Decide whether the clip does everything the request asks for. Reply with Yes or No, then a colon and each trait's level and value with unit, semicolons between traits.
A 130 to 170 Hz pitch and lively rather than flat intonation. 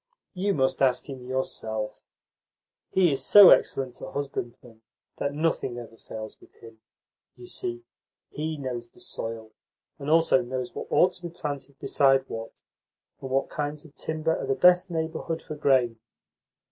No: low, 135 Hz; average, 4.7 semitones